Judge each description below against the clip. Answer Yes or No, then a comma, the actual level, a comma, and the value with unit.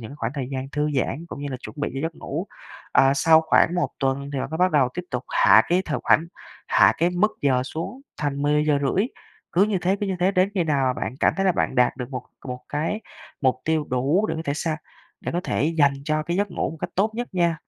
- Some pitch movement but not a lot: Yes, average, 4.5 semitones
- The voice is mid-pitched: Yes, medium, 155 Hz